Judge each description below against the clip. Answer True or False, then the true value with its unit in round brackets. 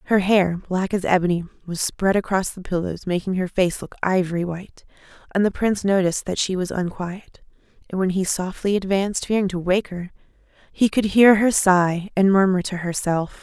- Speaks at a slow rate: False (190 wpm)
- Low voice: False (190 Hz)